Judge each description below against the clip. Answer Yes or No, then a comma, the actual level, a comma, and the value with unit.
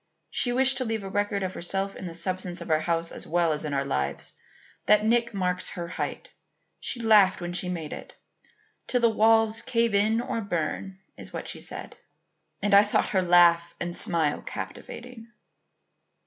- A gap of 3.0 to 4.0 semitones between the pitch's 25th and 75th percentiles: No, average, 4.5 semitones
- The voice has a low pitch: No, high, 195 Hz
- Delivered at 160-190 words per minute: Yes, average, 185 wpm